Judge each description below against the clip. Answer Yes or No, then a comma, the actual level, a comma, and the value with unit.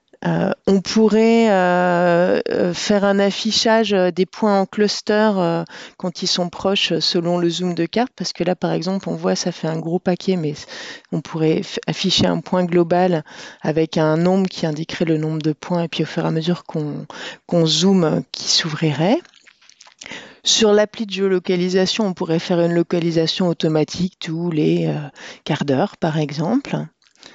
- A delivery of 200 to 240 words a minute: No, average, 170 wpm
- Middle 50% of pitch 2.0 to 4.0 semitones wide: Yes, average, 2.9 semitones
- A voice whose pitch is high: No, medium, 175 Hz